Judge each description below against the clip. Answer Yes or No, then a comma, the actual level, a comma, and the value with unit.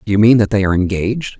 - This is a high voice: No, low, 105 Hz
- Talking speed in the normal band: No, fast, 300 wpm